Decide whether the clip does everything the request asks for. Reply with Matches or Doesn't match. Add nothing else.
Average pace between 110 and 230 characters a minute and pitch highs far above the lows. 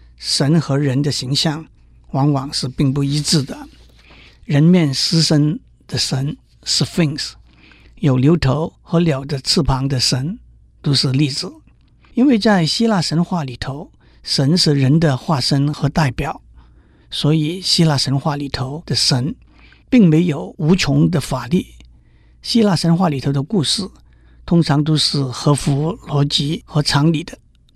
Doesn't match